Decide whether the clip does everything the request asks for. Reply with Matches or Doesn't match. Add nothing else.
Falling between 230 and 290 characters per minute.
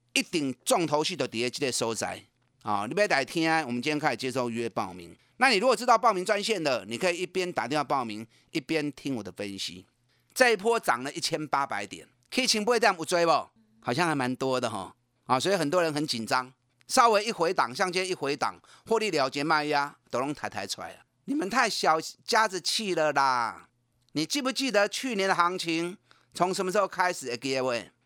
Doesn't match